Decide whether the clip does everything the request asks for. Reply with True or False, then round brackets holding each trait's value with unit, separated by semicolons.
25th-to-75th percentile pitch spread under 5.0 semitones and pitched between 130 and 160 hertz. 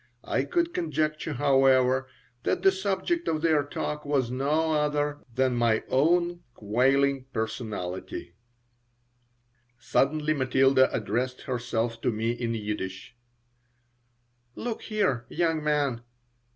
True (4.4 semitones; 135 Hz)